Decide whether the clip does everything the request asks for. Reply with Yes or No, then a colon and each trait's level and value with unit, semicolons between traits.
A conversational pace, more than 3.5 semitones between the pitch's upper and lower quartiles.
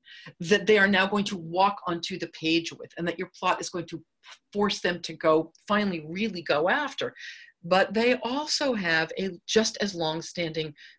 Yes: average, 190 wpm; average, 3.9 semitones